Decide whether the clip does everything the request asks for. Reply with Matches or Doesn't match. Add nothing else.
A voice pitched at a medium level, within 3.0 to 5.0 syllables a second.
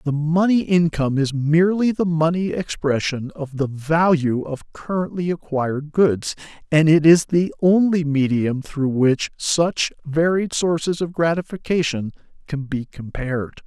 Matches